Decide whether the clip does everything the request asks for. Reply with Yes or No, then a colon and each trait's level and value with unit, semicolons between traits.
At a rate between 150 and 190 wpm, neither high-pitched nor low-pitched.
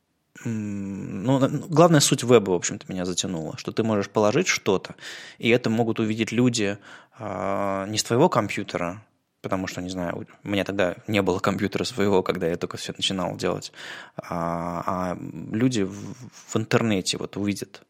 No: fast, 160 wpm; low, 100 Hz